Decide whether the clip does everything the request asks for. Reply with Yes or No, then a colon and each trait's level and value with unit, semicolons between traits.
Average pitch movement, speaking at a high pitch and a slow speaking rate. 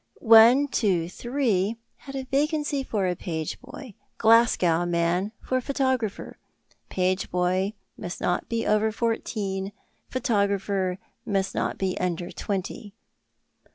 Yes: average, 4.5 semitones; high, 205 Hz; slow, 115 wpm